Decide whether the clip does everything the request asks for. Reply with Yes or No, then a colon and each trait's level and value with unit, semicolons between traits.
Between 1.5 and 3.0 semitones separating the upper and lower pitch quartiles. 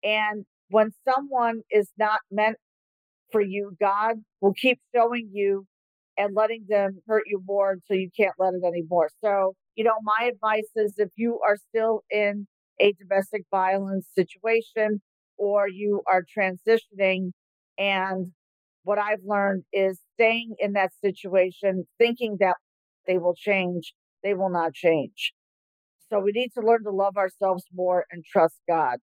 Yes: narrow, 2.4 semitones